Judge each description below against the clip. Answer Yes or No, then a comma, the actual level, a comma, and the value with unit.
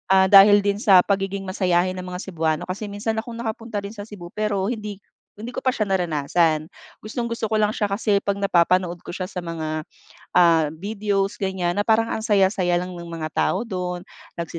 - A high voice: Yes, high, 195 Hz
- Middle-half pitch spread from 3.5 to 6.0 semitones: No, average, 3.1 semitones